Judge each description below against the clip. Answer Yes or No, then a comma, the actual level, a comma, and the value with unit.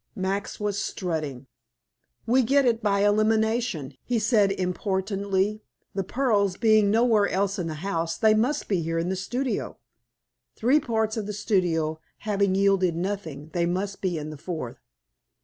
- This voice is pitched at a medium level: No, high, 200 Hz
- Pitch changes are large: No, average, 3.7 semitones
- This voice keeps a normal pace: Yes, average, 155 wpm